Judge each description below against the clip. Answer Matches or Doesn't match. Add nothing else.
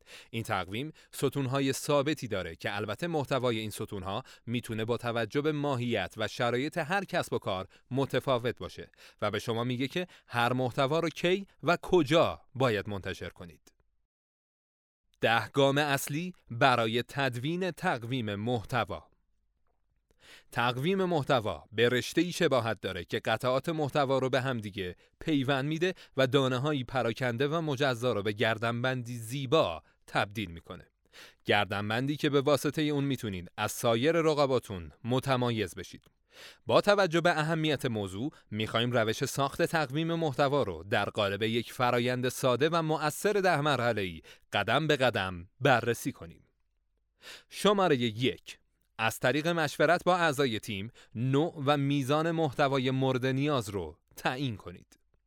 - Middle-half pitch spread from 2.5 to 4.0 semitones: Doesn't match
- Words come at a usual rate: Matches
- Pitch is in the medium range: Doesn't match